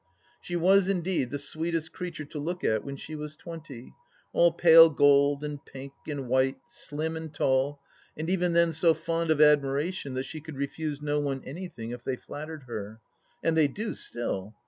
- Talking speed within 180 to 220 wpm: Yes, average, 185 wpm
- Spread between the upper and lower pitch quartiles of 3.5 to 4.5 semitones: No, average, 3.1 semitones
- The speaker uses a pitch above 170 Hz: No, medium, 150 Hz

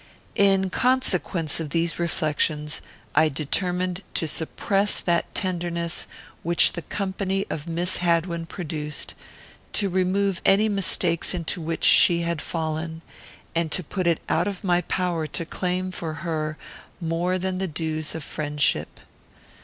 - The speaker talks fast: No, average, 140 wpm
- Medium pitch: Yes, medium, 170 Hz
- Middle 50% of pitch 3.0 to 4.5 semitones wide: No, narrow, 2.4 semitones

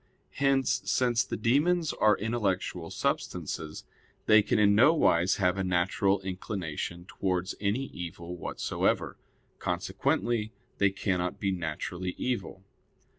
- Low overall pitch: Yes, very low, 95 Hz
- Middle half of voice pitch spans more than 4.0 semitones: Yes, average, 4.5 semitones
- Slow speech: Yes, slow, 120 wpm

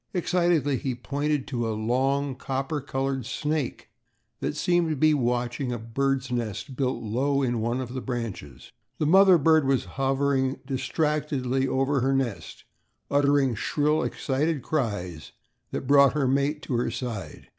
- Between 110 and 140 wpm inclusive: No, average, 150 wpm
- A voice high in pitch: No, low, 135 Hz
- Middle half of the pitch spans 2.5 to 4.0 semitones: Yes, average, 2.8 semitones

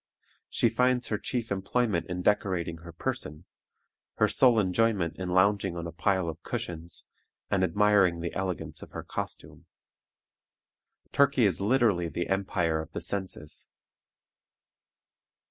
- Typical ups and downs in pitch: Yes, average, 3.9 semitones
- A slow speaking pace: Yes, slow, 130 wpm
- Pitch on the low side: Yes, very low, 95 Hz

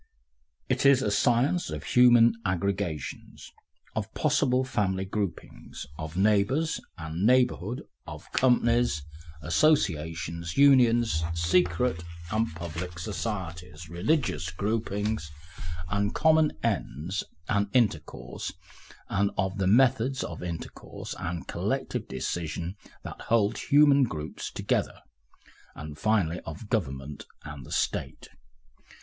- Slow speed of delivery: Yes, slow, 110 wpm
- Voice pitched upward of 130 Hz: No, low, 100 Hz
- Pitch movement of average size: No, wide, 6.3 semitones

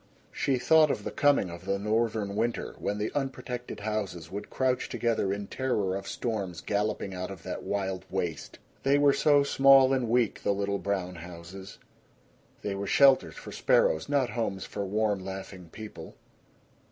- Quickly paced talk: No, average, 165 wpm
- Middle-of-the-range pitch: No, low, 105 Hz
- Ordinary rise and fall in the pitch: Yes, average, 4.5 semitones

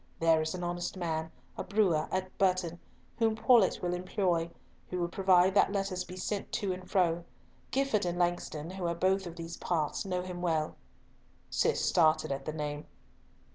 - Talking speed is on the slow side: No, average, 175 wpm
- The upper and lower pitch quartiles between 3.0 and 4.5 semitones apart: No, narrow, 2.4 semitones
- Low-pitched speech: No, medium, 180 Hz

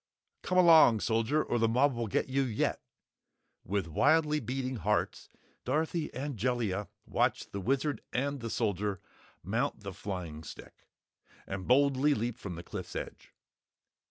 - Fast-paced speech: No, average, 145 wpm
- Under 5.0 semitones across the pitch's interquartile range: No, wide, 5.5 semitones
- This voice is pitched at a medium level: No, low, 120 Hz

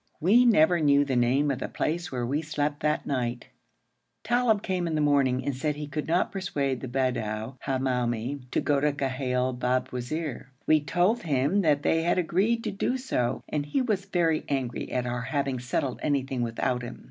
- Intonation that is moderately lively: Yes, average, 4.3 semitones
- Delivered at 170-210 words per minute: Yes, average, 190 wpm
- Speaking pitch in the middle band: Yes, medium, 145 Hz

